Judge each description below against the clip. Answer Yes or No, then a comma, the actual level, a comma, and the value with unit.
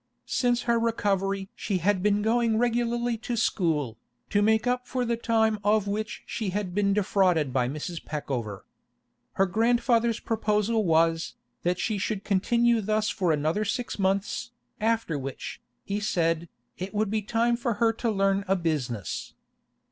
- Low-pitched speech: No, high, 205 Hz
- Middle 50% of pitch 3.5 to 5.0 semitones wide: Yes, average, 4.2 semitones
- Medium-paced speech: Yes, average, 155 wpm